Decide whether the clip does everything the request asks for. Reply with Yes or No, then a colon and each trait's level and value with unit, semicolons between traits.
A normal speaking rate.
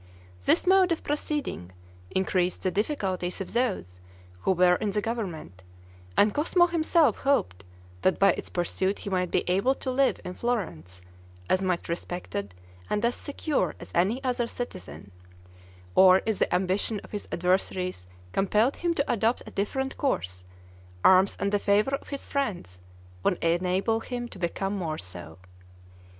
Yes: average, 155 wpm